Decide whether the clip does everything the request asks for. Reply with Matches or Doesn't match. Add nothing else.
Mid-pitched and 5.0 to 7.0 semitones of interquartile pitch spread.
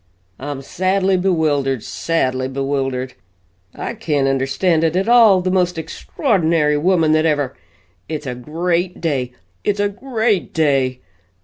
Matches